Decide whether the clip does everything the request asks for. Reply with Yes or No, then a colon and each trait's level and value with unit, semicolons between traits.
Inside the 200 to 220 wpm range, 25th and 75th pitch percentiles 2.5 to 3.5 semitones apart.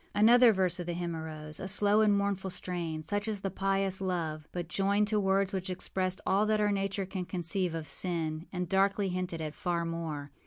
Yes: fast, 205 wpm; average, 2.8 semitones